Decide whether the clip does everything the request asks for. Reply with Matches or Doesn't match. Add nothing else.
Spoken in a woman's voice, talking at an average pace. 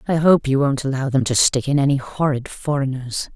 Doesn't match